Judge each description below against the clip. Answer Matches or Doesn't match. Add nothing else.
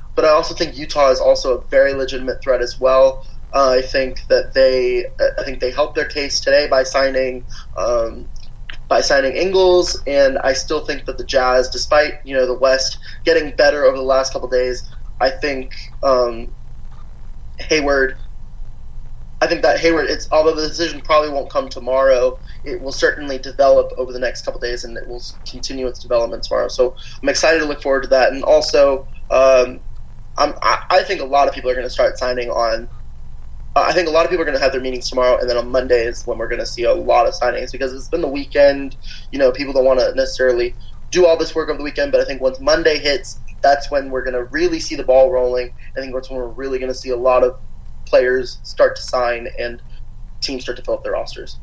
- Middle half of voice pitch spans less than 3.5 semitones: Matches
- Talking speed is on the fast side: Matches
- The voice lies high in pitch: Doesn't match